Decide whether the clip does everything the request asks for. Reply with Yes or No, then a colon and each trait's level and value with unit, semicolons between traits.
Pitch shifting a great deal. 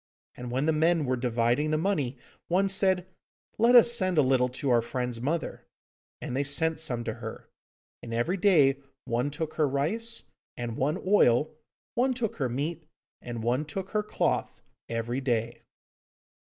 Yes: wide, 6.5 semitones